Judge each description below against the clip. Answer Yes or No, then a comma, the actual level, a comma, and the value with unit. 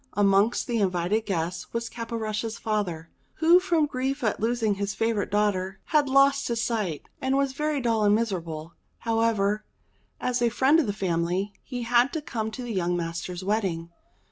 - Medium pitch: No, high, 220 Hz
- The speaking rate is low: No, average, 170 wpm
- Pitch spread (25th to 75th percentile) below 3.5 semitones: No, average, 4.2 semitones